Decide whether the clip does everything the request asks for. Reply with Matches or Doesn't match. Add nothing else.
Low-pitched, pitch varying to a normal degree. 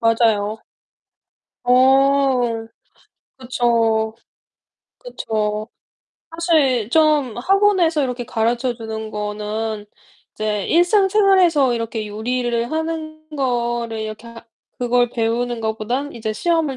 Doesn't match